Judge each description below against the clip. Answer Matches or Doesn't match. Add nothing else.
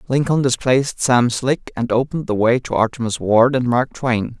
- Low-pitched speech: Matches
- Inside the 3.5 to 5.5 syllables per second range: Matches